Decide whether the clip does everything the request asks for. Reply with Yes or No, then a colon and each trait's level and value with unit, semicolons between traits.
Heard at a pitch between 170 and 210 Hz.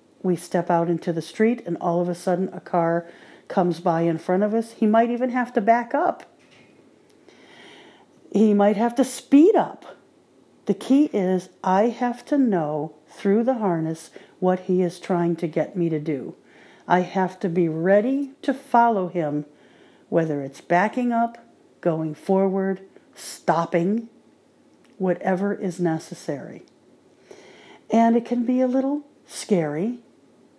Yes: high, 190 Hz